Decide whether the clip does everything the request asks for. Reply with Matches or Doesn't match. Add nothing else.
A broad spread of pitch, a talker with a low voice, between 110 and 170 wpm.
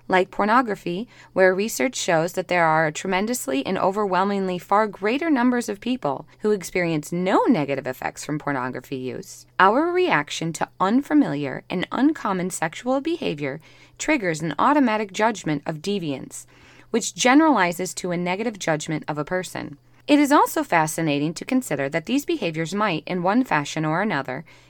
Doesn't match